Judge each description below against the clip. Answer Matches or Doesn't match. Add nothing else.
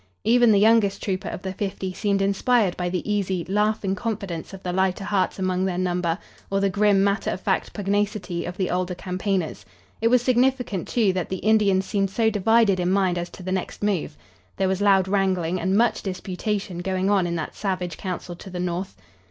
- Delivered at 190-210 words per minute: Matches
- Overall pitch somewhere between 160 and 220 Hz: Matches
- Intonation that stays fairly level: Matches